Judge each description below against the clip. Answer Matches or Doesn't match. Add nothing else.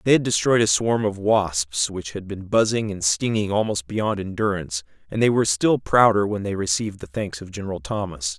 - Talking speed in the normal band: Doesn't match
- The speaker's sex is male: Matches